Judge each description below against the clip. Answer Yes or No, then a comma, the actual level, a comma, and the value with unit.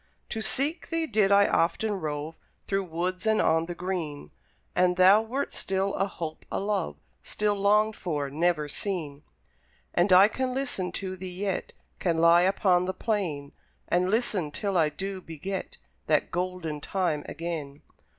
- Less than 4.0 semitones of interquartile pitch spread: Yes, average, 3.6 semitones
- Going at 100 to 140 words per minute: No, average, 160 wpm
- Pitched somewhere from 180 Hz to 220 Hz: Yes, medium, 185 Hz